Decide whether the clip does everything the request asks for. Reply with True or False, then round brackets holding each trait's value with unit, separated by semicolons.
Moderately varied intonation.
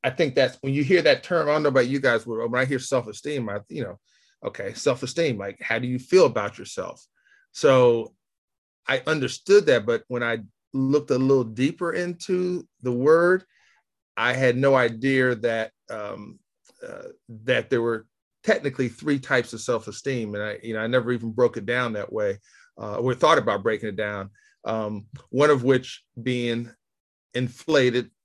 False (6.1 semitones)